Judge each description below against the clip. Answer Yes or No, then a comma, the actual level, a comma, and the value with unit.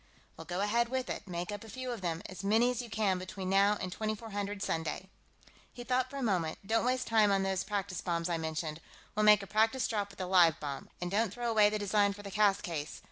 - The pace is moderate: No, fast, 245 wpm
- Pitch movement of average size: Yes, average, 3.3 semitones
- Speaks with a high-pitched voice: Yes, high, 200 Hz